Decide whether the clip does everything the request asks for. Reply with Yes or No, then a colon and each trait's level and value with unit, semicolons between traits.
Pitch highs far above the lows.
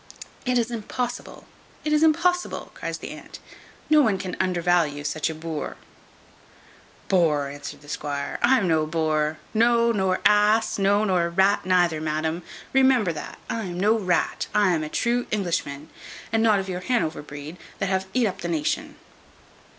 Yes: wide, 6.0 semitones